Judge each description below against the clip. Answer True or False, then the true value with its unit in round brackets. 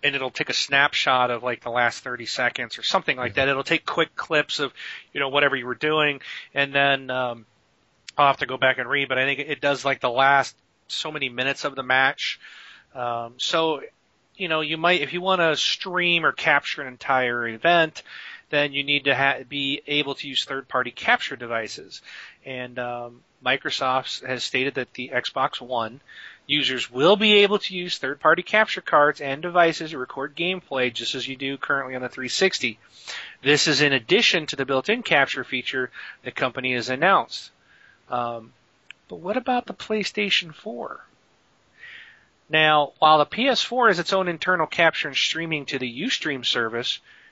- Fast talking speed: False (185 wpm)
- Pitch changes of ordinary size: True (4.2 semitones)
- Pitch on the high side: False (140 Hz)